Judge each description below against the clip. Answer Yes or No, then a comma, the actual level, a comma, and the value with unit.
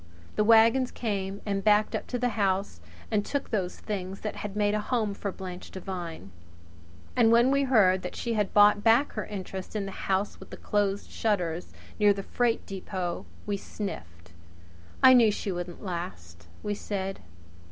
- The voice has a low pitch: No, high, 205 Hz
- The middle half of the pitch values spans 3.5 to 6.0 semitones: No, narrow, 2.5 semitones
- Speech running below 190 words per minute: Yes, average, 175 wpm